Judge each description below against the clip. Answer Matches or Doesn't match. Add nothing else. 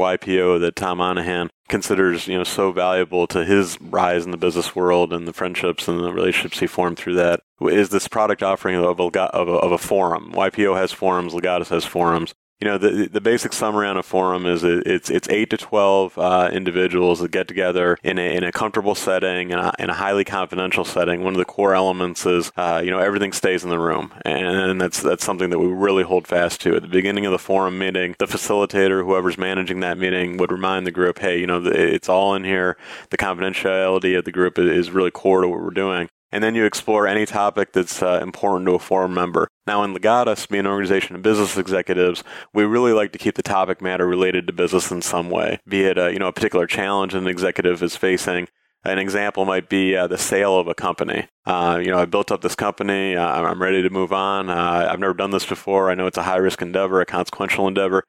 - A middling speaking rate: Doesn't match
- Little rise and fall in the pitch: Matches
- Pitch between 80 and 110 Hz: Matches